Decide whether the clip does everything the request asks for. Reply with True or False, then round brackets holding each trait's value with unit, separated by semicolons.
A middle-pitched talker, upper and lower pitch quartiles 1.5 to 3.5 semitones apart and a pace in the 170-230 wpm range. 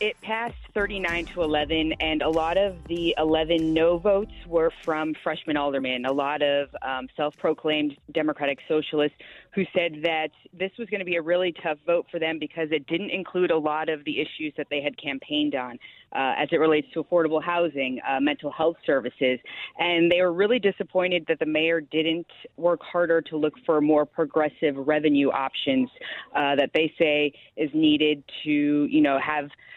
True (160 Hz; 2.4 semitones; 185 wpm)